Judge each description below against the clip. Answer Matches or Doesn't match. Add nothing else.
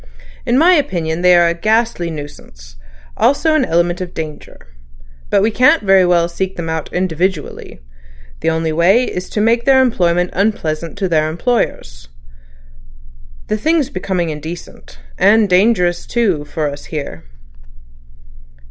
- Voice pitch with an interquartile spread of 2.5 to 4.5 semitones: Doesn't match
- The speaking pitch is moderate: Matches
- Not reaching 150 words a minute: Matches